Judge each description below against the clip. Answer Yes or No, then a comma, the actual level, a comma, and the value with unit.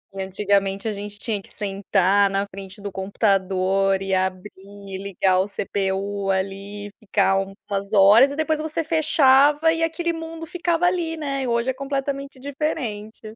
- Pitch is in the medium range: No, high, 205 Hz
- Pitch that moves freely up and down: Yes, wide, 6.3 semitones